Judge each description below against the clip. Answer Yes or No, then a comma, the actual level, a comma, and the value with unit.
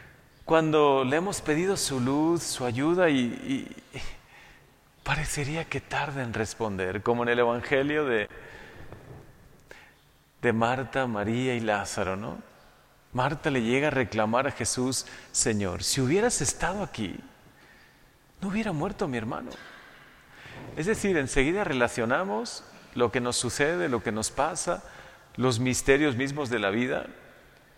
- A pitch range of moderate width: Yes, average, 4.2 semitones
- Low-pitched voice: Yes, low, 130 Hz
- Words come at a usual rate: Yes, average, 135 wpm